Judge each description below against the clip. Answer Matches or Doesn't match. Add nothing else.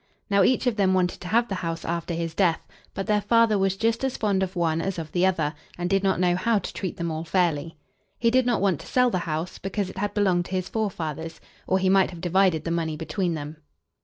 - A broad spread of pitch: Doesn't match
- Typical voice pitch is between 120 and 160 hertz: Doesn't match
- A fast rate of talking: Matches